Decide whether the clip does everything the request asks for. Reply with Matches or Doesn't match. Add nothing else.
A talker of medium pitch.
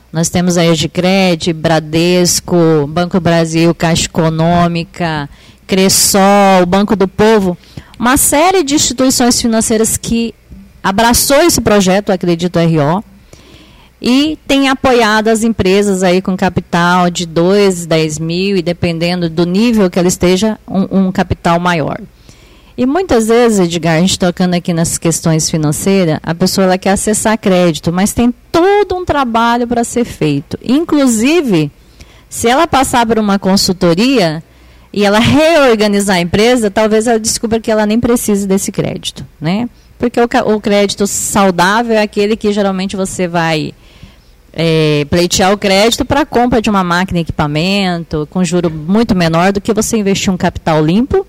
Doesn't match